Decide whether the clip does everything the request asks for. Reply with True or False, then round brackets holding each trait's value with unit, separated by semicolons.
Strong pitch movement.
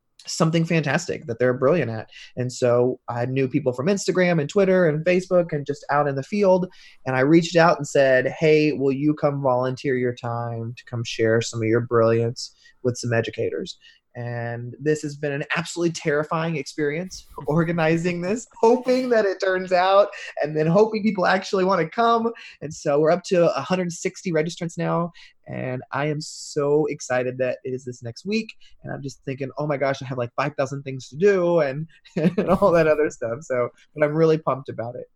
True (5.7 semitones)